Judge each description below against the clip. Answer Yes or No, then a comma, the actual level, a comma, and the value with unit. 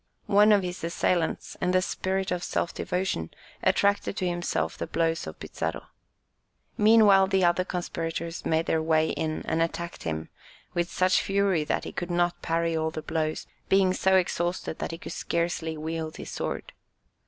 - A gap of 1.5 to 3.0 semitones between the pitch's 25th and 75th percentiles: Yes, narrow, 2.5 semitones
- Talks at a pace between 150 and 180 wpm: Yes, average, 170 wpm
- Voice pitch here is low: No, medium, 175 Hz